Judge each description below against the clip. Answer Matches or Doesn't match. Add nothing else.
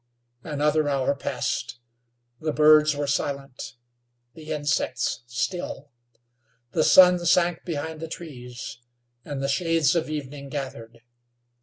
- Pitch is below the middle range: Doesn't match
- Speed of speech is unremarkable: Doesn't match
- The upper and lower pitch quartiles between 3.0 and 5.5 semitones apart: Doesn't match